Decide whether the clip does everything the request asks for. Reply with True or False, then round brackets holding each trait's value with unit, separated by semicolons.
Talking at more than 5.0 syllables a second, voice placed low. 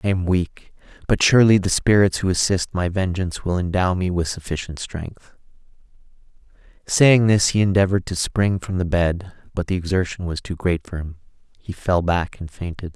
True (5.2 syllables/s; 90 Hz)